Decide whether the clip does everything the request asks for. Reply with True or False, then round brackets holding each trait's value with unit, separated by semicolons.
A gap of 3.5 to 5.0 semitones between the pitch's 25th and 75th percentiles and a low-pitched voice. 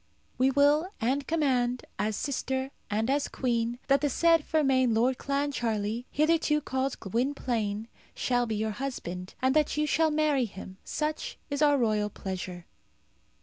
False (4.5 semitones; 260 Hz)